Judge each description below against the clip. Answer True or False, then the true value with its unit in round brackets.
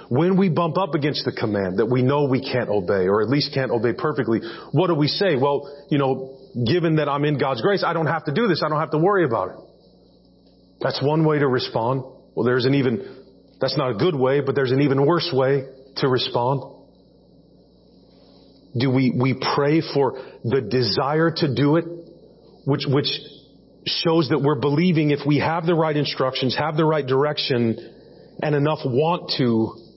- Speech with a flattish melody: False (3.3 semitones)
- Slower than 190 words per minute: False (195 wpm)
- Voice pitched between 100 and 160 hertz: True (140 Hz)